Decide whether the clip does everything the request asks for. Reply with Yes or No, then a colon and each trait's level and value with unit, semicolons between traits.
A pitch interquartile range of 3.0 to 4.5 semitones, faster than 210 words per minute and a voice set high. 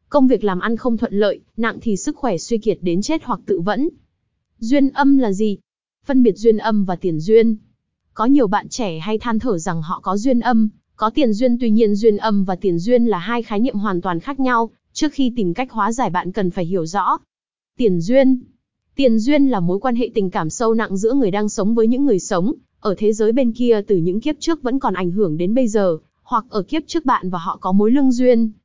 Yes: average, 4.1 semitones; average, 245 wpm; high, 220 Hz